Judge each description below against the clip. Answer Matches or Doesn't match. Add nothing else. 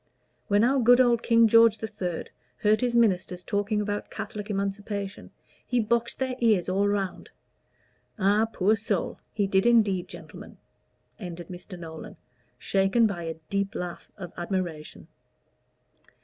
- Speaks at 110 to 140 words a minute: Matches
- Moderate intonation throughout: Matches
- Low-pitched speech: Doesn't match